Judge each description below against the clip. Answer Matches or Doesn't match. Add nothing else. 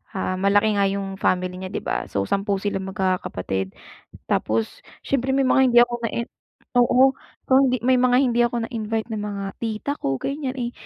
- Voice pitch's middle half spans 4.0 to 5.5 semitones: Matches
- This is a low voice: Doesn't match